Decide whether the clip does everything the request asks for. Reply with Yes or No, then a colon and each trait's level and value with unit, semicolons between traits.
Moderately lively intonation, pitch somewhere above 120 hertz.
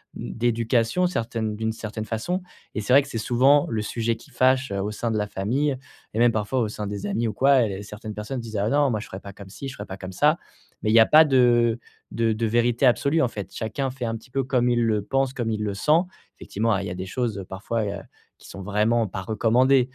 No: average, 3.4 semitones; low, 115 Hz